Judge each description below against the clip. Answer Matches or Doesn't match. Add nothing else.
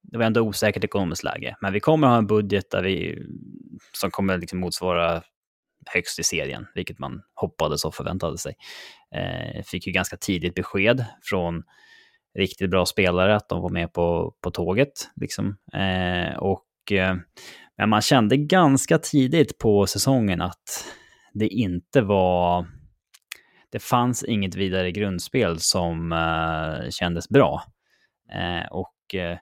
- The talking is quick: Doesn't match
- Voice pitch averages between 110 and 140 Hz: Doesn't match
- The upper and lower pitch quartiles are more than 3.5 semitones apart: Matches